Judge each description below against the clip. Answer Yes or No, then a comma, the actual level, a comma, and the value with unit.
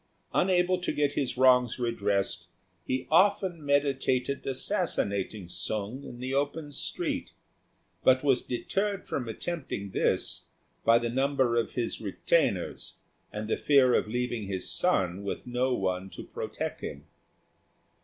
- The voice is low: Yes, low, 125 Hz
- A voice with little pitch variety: No, average, 4.7 semitones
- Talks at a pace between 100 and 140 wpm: Yes, slow, 135 wpm